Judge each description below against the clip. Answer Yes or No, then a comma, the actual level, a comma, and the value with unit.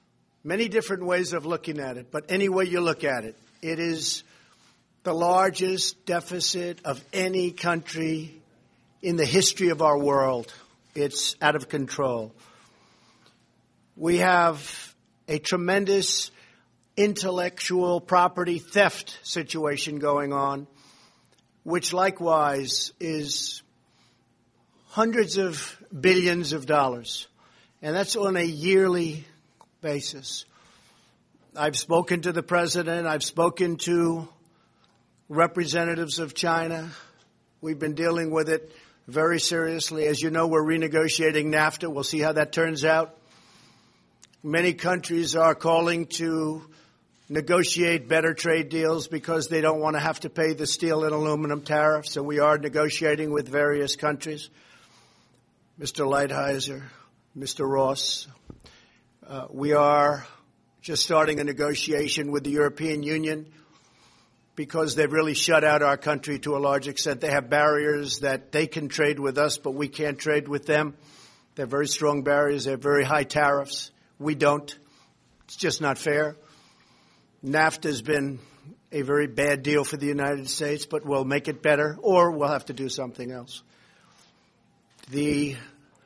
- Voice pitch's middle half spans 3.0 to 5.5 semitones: No, narrow, 2.5 semitones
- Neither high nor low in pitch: Yes, medium, 155 Hz